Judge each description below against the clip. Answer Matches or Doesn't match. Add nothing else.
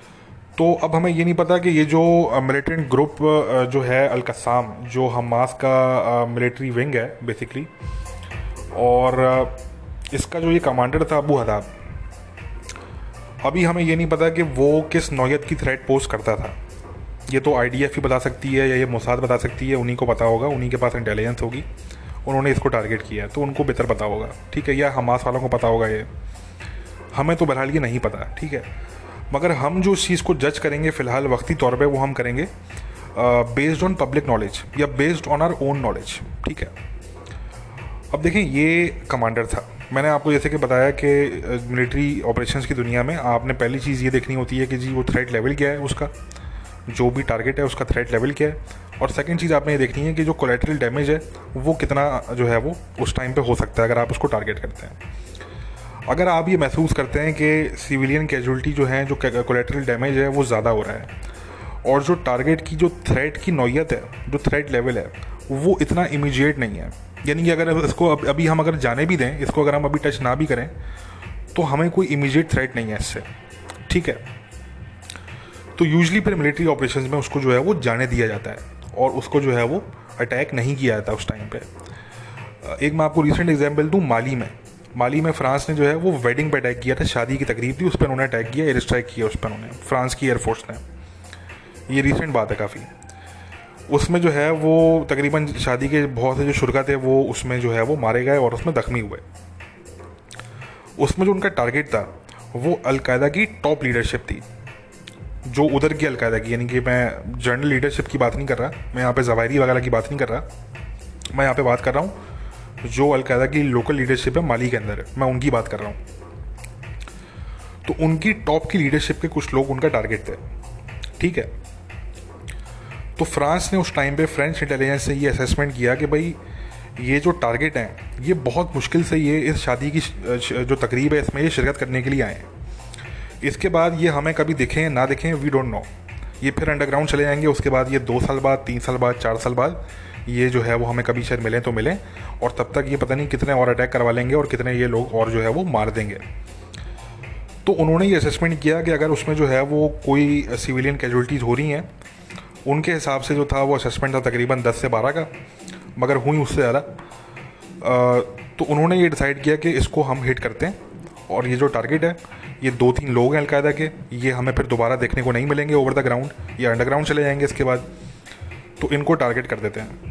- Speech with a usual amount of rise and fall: Matches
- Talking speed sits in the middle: Doesn't match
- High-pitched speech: Doesn't match